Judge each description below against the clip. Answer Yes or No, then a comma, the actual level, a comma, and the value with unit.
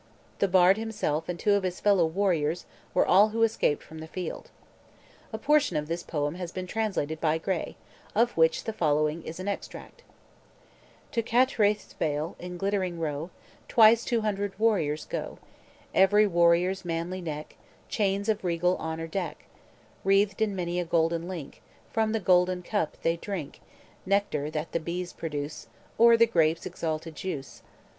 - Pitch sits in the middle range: Yes, medium, 180 Hz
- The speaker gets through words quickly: No, average, 160 wpm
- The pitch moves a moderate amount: Yes, average, 3.9 semitones